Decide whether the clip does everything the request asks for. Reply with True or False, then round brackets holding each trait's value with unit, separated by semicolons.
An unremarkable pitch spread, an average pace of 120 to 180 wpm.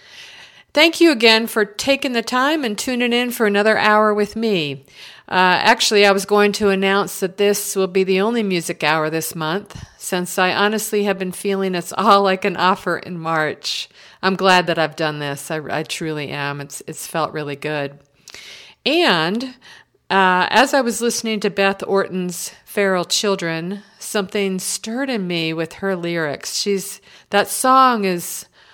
True (3.9 semitones; 170 wpm)